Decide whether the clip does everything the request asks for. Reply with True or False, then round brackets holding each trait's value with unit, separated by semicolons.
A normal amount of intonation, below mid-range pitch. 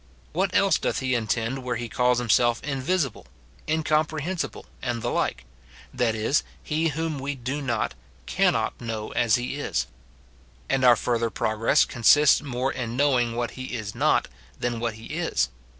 True (3.3 semitones; 125 Hz)